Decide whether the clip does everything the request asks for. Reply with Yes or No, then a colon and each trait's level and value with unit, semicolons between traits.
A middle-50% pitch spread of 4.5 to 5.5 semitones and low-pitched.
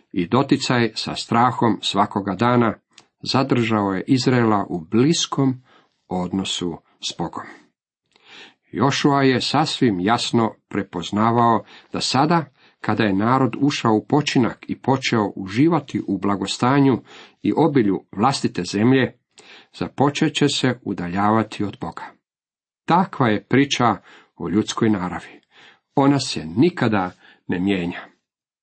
Yes: average, 4.9 semitones; low, 115 Hz